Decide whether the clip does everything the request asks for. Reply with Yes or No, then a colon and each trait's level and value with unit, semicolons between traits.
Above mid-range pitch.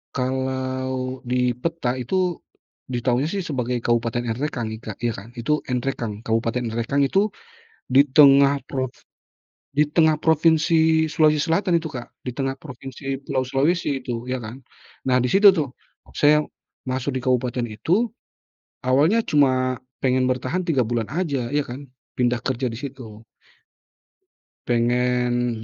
No: low, 130 Hz